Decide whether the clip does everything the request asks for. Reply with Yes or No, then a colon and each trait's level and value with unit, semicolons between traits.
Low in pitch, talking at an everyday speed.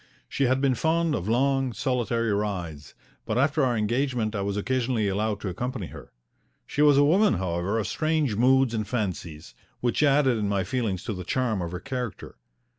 Yes: low, 115 Hz; average, 190 wpm